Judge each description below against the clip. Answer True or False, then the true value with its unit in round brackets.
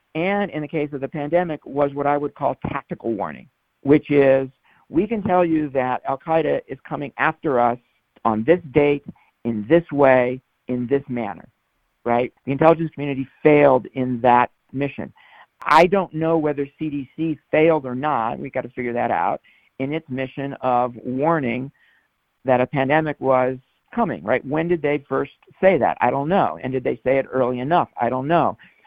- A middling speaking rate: True (185 wpm)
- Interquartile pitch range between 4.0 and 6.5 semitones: False (3.5 semitones)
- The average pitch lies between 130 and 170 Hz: True (140 Hz)